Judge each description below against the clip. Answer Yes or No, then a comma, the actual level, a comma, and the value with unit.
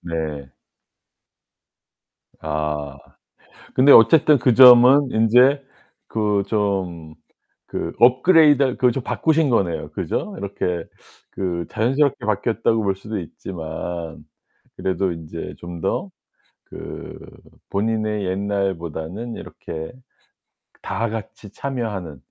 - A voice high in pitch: No, low, 100 Hz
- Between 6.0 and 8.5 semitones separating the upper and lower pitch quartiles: Yes, wide, 6.3 semitones